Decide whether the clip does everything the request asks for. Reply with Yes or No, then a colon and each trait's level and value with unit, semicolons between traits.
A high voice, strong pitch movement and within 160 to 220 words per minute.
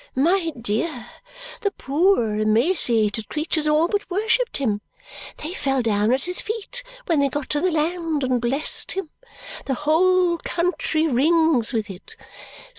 No: very high, 300 Hz; wide, 6.3 semitones; average, 145 wpm